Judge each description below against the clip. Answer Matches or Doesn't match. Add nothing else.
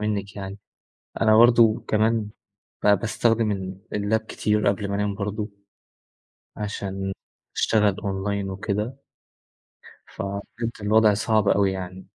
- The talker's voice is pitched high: Doesn't match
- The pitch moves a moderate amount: Doesn't match